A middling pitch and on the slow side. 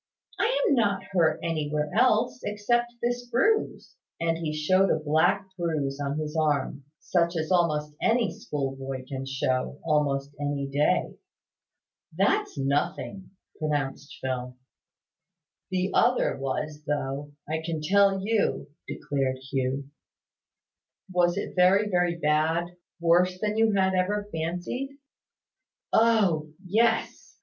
Yes: medium, 165 Hz; slow, 120 wpm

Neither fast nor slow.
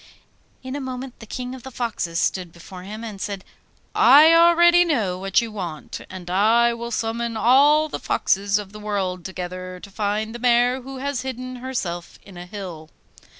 Yes: average, 180 wpm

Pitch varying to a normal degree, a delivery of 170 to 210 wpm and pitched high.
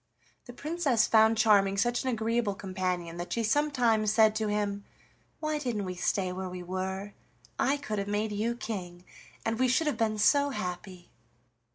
Yes: average, 3.9 semitones; average, 175 wpm; high, 215 Hz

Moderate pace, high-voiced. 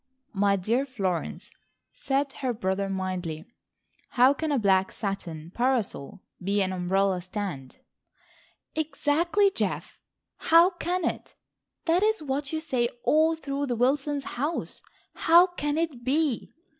No: slow, 130 wpm; very high, 260 Hz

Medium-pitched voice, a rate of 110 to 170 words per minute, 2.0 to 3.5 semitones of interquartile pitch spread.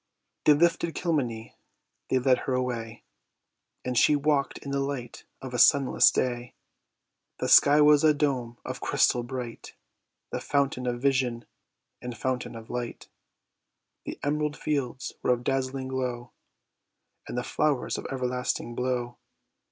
No: low, 130 Hz; average, 140 wpm; narrow, 2.5 semitones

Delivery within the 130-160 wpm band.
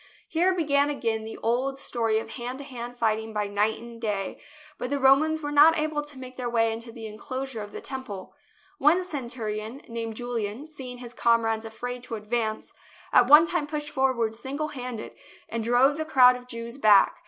No: average, 190 wpm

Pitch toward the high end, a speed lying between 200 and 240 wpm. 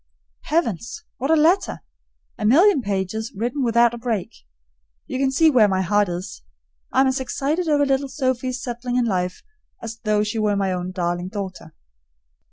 No: high, 230 Hz; average, 170 wpm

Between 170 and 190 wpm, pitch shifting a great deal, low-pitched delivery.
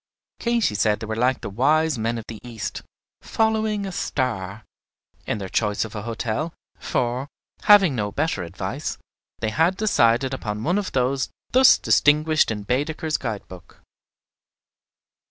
No: average, 150 wpm; wide, 6.7 semitones; low, 125 Hz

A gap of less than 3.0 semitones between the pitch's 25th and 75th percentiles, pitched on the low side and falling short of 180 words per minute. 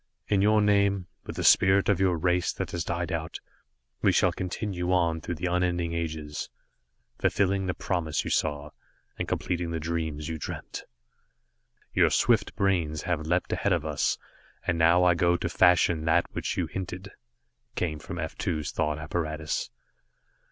Yes: narrow, 2.5 semitones; very low, 85 Hz; average, 165 wpm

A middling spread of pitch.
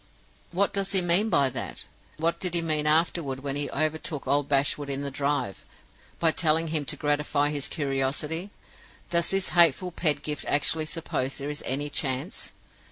Yes: average, 3.0 semitones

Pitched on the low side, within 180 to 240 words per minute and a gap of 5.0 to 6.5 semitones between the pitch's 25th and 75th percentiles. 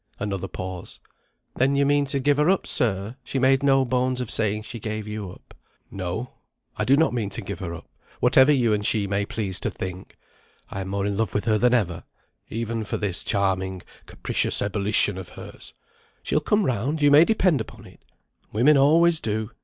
Yes: low, 110 Hz; average, 200 wpm; wide, 5.4 semitones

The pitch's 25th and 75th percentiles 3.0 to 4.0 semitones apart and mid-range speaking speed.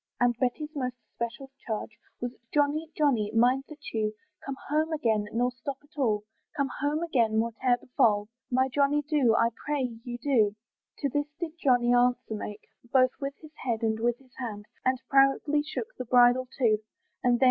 Yes: average, 3.6 semitones; average, 180 wpm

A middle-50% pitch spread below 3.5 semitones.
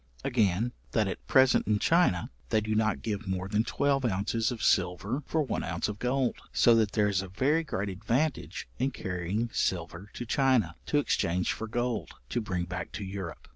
No: average, 4.6 semitones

